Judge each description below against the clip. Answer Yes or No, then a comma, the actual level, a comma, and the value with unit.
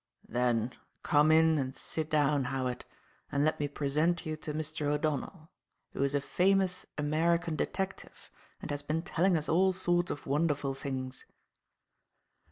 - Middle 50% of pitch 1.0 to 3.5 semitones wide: Yes, average, 3.1 semitones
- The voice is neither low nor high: Yes, medium, 155 Hz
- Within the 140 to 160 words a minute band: Yes, average, 150 wpm